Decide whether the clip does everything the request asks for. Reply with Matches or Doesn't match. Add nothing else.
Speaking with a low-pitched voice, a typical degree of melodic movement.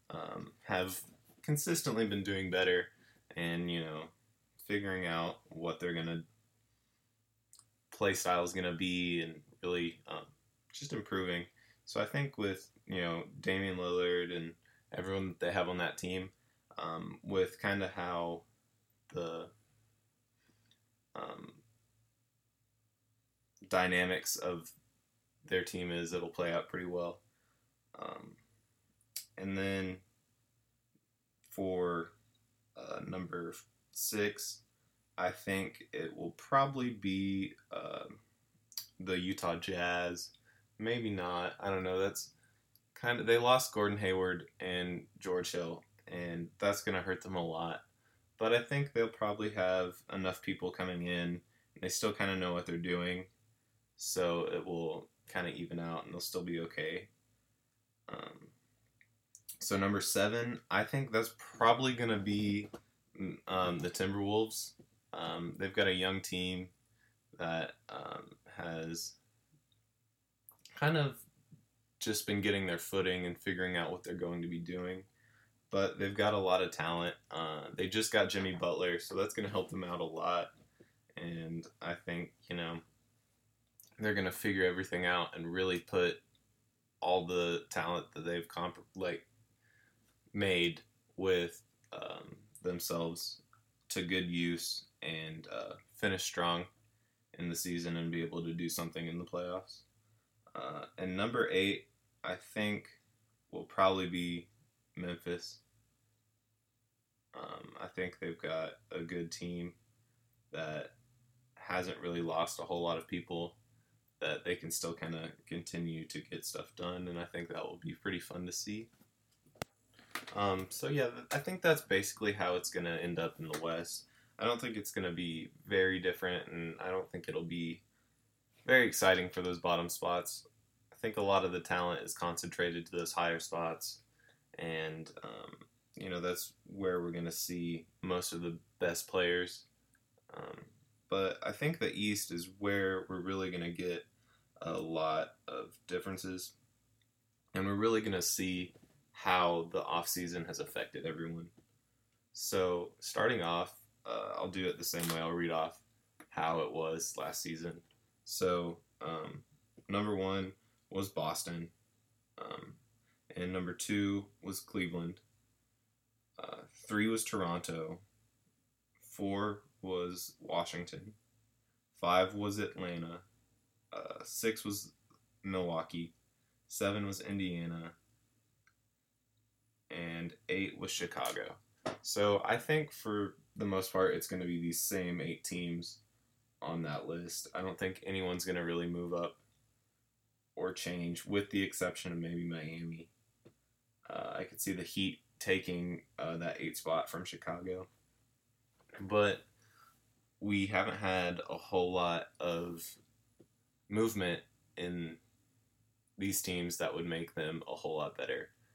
Matches